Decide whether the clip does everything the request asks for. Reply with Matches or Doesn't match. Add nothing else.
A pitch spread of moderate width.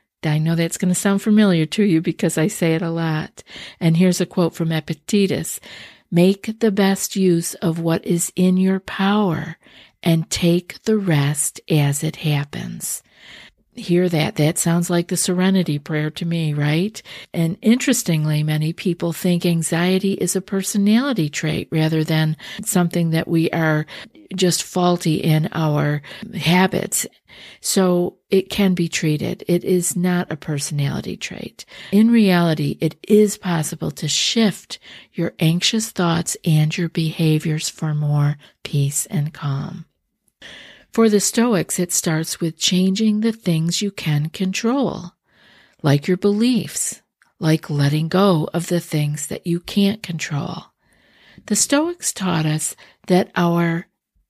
Matches